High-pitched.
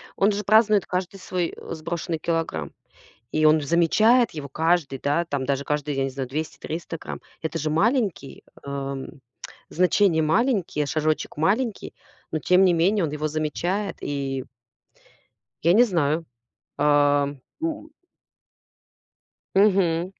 No: medium, 165 Hz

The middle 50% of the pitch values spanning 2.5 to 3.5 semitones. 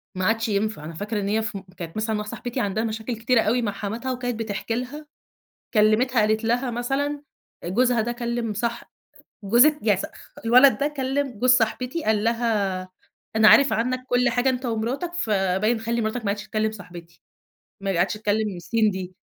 Yes: average, 2.8 semitones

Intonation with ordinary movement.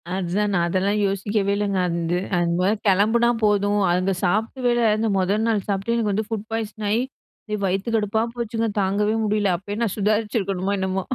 No: narrow, 2.3 semitones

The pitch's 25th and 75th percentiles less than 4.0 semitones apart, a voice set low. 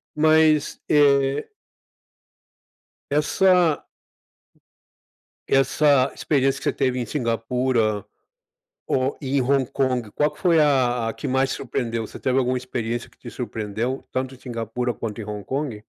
Yes: average, 3.1 semitones; low, 130 Hz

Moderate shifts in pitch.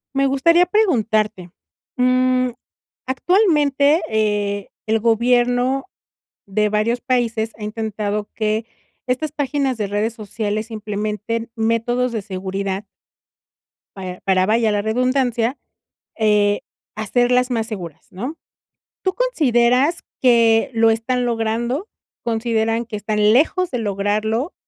Yes: average, 3.1 semitones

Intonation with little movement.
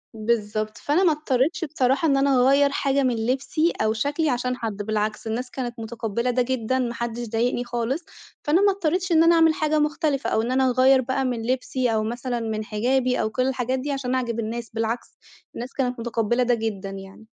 No: average, 3.2 semitones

